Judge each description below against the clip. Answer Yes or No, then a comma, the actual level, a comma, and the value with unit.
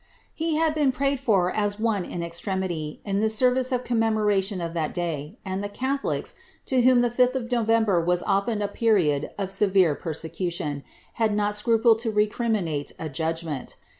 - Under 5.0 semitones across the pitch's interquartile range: No, wide, 5.4 semitones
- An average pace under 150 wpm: No, average, 170 wpm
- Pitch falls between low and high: No, high, 205 Hz